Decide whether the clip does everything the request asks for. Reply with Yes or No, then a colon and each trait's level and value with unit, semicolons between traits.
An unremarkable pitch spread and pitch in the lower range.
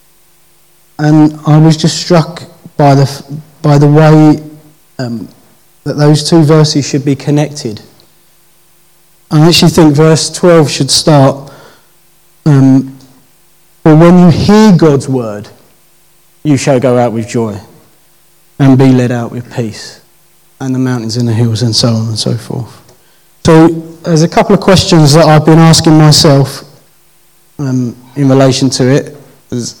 No: average, 4.3 semitones; medium, 150 Hz